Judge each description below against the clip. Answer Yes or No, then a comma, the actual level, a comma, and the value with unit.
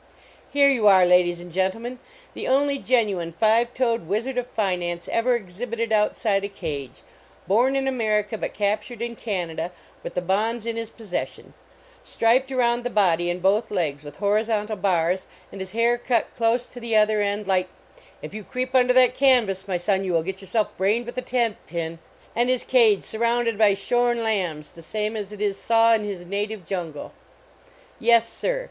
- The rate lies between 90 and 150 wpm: No, average, 185 wpm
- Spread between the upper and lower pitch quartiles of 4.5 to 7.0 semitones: No, average, 4.0 semitones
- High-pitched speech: Yes, high, 215 Hz